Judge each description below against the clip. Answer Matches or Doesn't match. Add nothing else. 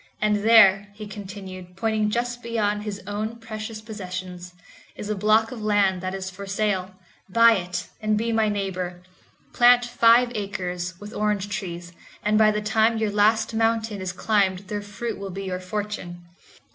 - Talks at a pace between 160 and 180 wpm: Matches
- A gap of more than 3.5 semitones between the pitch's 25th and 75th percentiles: Doesn't match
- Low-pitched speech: Doesn't match